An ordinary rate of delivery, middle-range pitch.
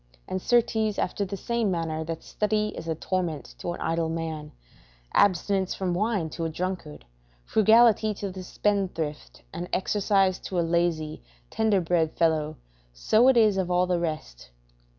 Yes: average, 160 wpm; medium, 180 Hz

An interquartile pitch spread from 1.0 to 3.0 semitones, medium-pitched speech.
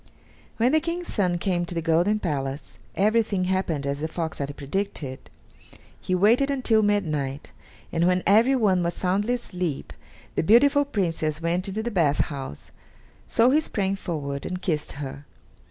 No: wide, 5.6 semitones; medium, 180 Hz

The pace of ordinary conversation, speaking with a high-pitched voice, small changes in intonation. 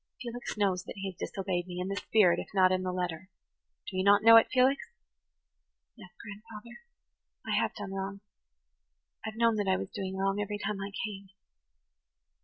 Yes: average, 180 wpm; high, 195 Hz; narrow, 2.2 semitones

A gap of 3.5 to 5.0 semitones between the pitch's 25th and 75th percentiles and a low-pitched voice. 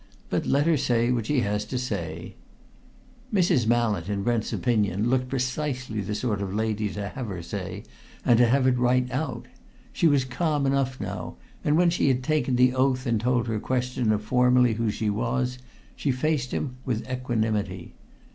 No: average, 3.1 semitones; low, 125 Hz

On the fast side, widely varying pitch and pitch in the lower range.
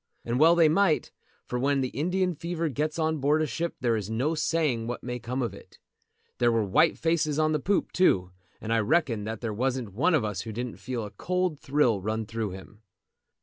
Yes: fast, 220 wpm; wide, 5.8 semitones; low, 130 Hz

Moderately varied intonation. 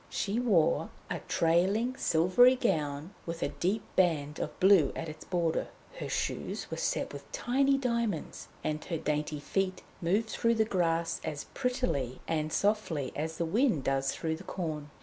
No: wide, 6.1 semitones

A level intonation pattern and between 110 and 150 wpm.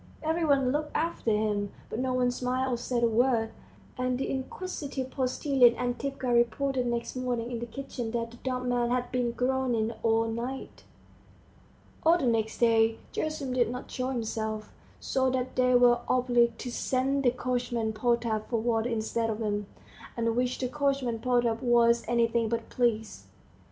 No: narrow, 2.0 semitones; average, 165 wpm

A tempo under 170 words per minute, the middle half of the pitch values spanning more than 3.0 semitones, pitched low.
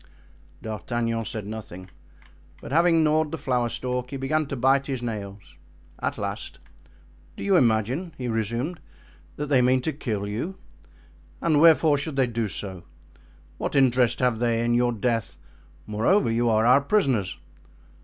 Yes: average, 155 wpm; average, 4.2 semitones; low, 125 Hz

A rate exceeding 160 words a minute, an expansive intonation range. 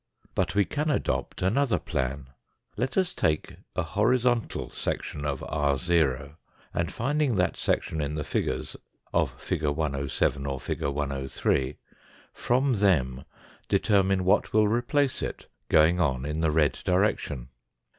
No: slow, 135 wpm; wide, 7.2 semitones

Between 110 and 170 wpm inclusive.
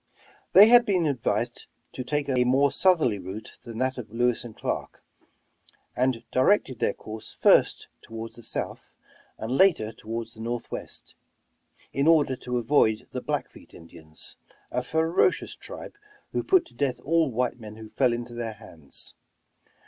Yes: average, 155 wpm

